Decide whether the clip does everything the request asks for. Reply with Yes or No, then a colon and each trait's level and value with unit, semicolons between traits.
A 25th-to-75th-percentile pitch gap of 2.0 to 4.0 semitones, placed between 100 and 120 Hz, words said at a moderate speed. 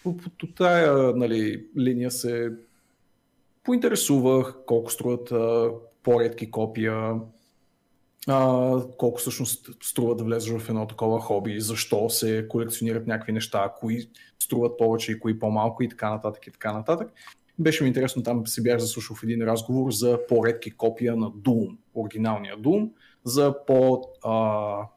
Yes: narrow, 2.4 semitones; low, 115 Hz; average, 135 wpm